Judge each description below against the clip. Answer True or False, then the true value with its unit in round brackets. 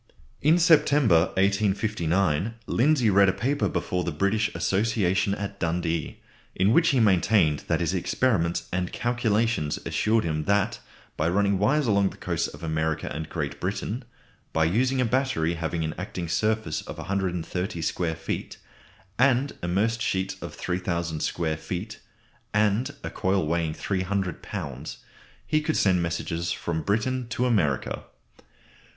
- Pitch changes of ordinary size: True (4.8 semitones)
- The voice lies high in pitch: False (95 Hz)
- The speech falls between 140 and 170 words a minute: True (145 wpm)